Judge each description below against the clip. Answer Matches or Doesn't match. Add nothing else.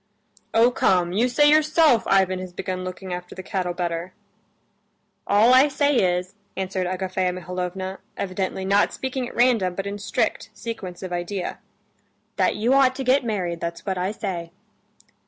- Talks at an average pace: Matches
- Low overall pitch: Doesn't match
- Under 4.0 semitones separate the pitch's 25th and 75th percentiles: Doesn't match